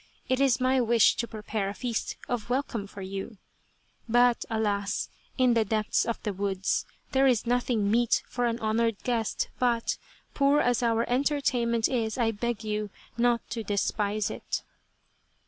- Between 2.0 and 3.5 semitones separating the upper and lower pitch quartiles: Yes, narrow, 2.5 semitones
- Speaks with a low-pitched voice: No, high, 230 Hz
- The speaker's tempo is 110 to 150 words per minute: No, average, 160 wpm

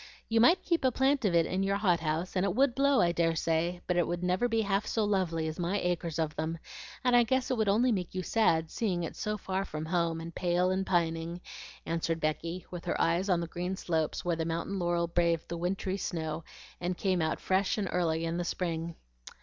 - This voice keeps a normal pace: No, fast, 235 wpm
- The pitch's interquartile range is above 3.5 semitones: No, average, 3.0 semitones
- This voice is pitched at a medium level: Yes, medium, 175 Hz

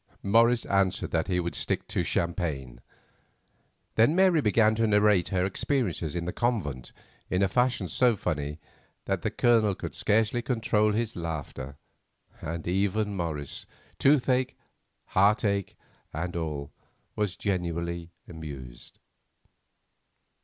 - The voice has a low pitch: Yes, very low, 95 Hz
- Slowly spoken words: Yes, slow, 120 wpm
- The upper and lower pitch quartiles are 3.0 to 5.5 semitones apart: Yes, average, 5.0 semitones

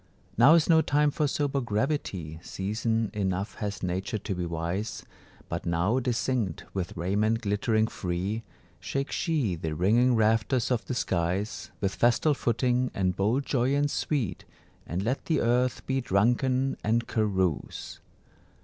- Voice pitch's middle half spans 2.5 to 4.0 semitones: No, average, 5.1 semitones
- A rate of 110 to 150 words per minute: Yes, average, 140 wpm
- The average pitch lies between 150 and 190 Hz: No, low, 110 Hz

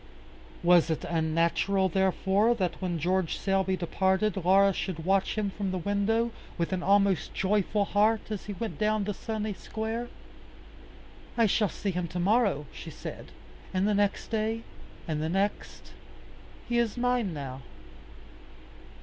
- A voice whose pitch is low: No, high, 195 Hz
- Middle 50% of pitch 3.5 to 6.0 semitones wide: No, average, 3.0 semitones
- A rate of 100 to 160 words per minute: Yes, average, 150 wpm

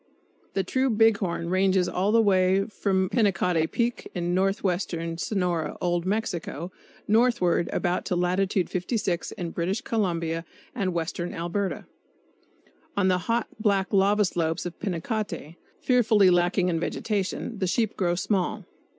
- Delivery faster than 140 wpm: No, slow, 135 wpm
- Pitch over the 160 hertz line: Yes, medium, 185 Hz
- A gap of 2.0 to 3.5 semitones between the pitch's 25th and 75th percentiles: Yes, average, 2.9 semitones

